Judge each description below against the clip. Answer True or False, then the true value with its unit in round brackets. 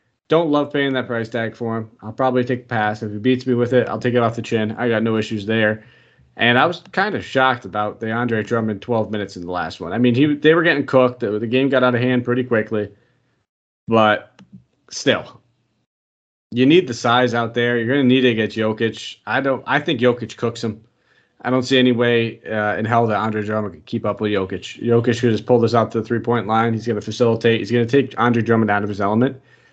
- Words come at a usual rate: False (250 wpm)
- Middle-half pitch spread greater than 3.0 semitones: False (2.4 semitones)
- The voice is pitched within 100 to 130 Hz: True (115 Hz)